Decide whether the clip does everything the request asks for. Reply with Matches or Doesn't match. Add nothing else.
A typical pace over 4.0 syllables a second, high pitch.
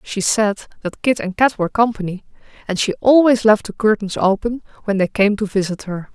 Matches